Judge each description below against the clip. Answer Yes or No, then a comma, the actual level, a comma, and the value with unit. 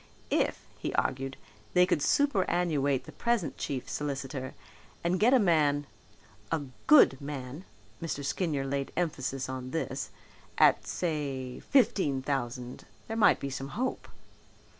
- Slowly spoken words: Yes, slow, 130 wpm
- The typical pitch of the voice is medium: Yes, medium, 145 Hz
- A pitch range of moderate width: Yes, average, 4.8 semitones